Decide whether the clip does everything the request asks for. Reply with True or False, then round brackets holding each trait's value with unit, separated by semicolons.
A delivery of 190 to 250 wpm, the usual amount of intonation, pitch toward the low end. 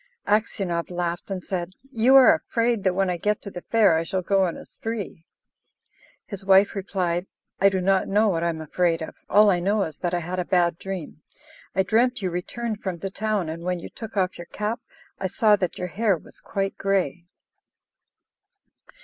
False (200 wpm; 3.0 semitones; 190 Hz)